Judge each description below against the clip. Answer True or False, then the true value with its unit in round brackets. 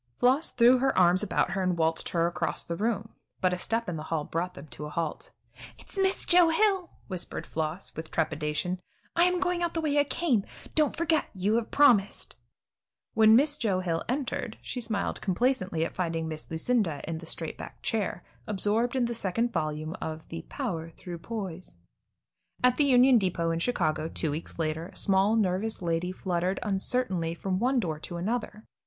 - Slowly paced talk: False (190 wpm)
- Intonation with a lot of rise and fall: True (6.8 semitones)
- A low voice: False (190 Hz)